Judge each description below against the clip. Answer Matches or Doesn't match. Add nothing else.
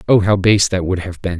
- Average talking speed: Doesn't match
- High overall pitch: Doesn't match